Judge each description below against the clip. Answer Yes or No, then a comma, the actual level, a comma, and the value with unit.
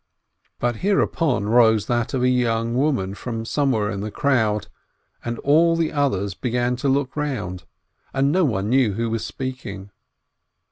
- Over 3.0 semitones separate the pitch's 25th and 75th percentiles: Yes, average, 4.2 semitones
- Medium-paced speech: Yes, average, 160 wpm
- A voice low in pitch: Yes, low, 120 Hz